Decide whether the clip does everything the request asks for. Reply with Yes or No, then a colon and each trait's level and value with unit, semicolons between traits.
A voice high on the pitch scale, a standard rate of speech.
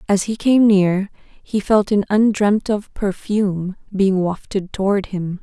Yes: high, 200 Hz; average, 155 wpm